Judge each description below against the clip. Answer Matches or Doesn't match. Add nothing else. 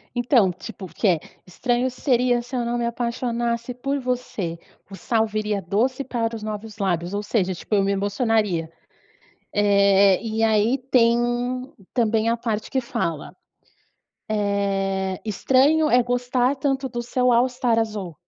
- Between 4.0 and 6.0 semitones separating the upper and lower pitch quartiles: Doesn't match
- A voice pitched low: Doesn't match